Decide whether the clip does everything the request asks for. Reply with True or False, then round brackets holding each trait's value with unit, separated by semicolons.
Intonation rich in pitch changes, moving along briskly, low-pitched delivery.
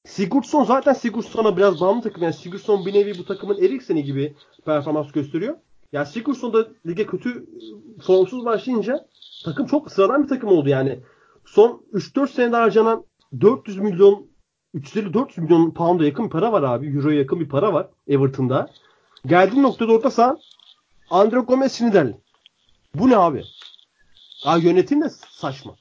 False (7.7 semitones; 145 wpm; 205 Hz)